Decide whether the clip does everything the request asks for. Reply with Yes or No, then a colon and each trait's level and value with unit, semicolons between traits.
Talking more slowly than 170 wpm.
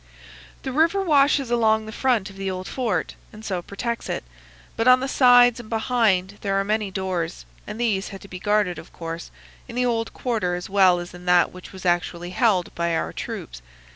No: fast, 205 wpm